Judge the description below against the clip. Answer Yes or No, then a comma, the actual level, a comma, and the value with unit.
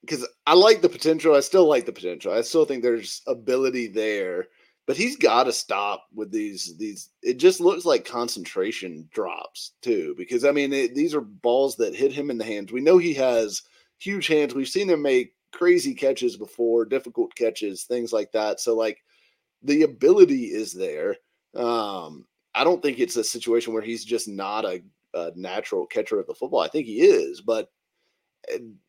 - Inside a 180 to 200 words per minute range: Yes, average, 190 wpm